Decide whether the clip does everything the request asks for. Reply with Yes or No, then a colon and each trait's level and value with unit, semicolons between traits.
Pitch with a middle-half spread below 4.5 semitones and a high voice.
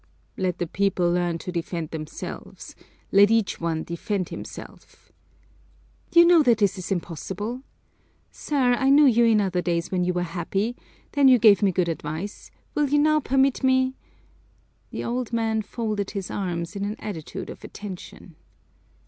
No: wide, 5.5 semitones; high, 200 Hz